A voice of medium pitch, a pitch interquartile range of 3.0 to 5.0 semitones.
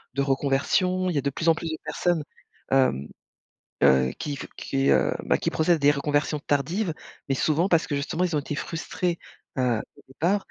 Yes: medium, 145 Hz; average, 3.7 semitones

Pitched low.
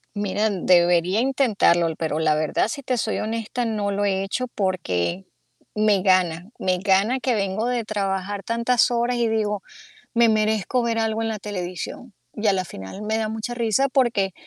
No: high, 210 Hz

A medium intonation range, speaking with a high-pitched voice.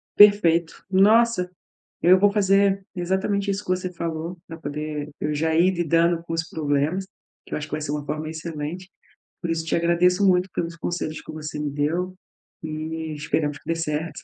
No: average, 3.0 semitones; medium, 165 Hz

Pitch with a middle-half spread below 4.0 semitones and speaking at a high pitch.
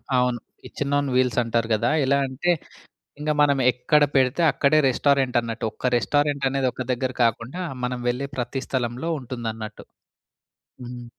No: narrow, 2.6 semitones; low, 130 Hz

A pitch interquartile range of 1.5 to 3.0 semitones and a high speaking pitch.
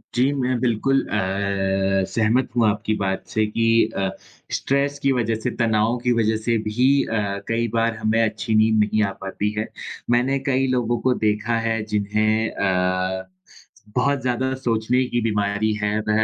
No: narrow, 2.6 semitones; low, 110 Hz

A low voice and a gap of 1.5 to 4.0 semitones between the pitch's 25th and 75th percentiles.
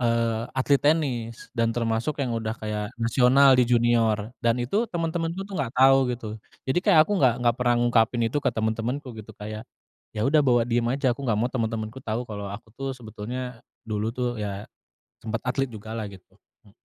Yes: low, 120 Hz; average, 2.9 semitones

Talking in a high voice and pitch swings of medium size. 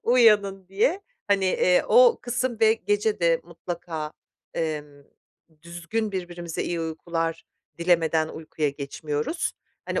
No: medium, 175 Hz; average, 4.5 semitones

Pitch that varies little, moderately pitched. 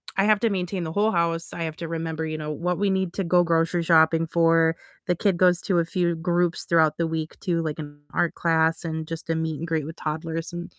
Yes: narrow, 1.5 semitones; medium, 165 Hz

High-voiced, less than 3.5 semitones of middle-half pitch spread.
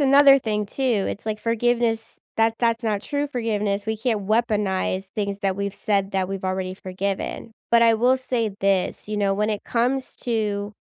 Yes: high, 215 Hz; average, 2.8 semitones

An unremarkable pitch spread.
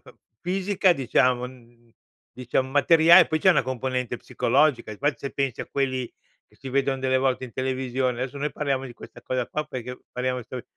No: narrow, 1.9 semitones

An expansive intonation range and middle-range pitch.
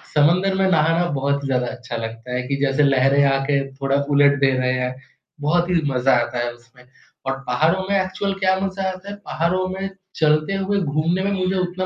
Yes: wide, 5.7 semitones; medium, 150 Hz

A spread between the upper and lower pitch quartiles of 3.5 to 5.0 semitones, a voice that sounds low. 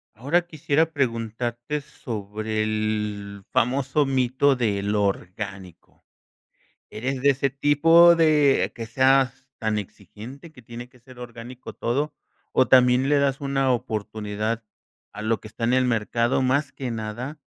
Yes: average, 4.0 semitones; low, 125 Hz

